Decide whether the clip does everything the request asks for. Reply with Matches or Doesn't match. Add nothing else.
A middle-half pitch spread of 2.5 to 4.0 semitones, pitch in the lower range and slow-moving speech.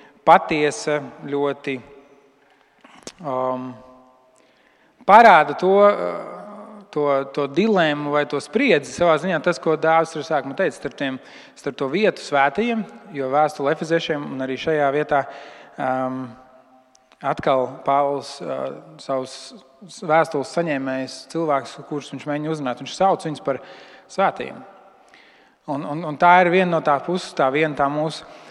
Doesn't match